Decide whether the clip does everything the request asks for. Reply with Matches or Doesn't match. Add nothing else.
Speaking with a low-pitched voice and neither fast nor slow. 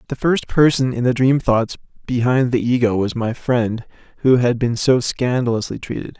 Matches